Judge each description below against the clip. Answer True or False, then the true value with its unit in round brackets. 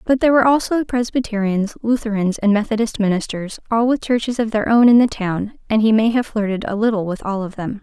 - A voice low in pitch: False (220 Hz)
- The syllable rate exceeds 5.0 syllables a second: True (6.0 syllables/s)